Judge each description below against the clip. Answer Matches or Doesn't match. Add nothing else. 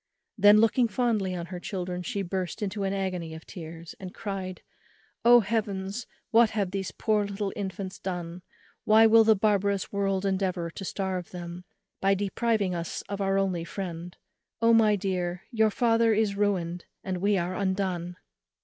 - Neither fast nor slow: Matches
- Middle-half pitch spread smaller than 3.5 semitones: Matches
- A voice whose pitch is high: Matches